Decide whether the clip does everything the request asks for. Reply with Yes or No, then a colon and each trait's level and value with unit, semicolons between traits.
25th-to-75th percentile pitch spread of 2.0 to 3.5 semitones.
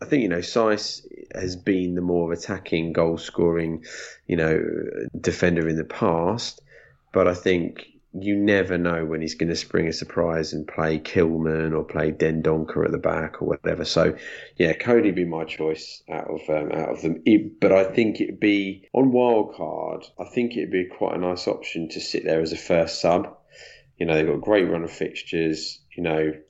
Yes: narrow, 2.5 semitones